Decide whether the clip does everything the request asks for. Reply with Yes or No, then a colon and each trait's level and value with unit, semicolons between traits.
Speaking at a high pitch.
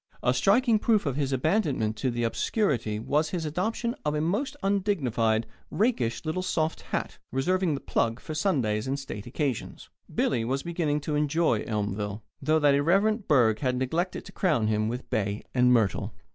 No: medium, 145 Hz